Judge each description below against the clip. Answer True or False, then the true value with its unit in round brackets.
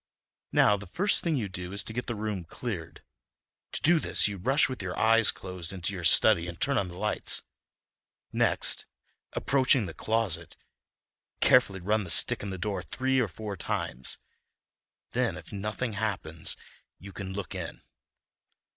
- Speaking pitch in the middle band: False (100 Hz)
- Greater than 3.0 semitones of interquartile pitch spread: True (4.0 semitones)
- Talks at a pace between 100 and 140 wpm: False (160 wpm)